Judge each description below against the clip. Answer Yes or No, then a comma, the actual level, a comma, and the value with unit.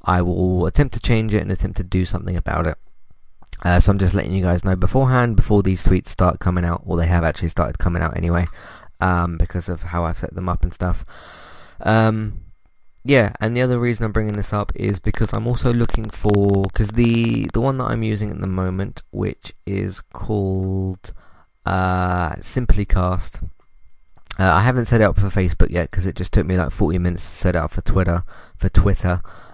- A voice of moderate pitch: No, very low, 95 Hz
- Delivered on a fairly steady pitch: No, average, 3.2 semitones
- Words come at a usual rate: No, fast, 210 wpm